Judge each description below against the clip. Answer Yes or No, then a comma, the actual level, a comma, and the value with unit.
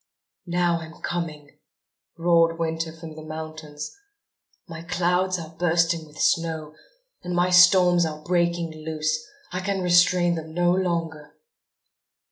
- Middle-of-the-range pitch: Yes, medium, 165 Hz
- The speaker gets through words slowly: Yes, slow, 125 wpm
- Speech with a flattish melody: Yes, narrow, 1.8 semitones